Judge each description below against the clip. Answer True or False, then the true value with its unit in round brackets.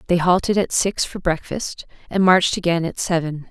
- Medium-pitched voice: True (175 Hz)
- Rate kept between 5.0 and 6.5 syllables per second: True (5.2 syllables/s)